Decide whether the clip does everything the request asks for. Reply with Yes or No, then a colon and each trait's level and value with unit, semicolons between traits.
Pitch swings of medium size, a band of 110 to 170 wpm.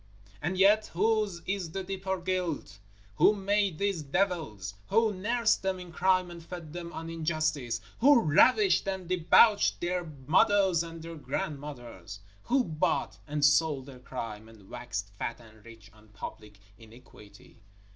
No: wide, 7.1 semitones; average, 150 wpm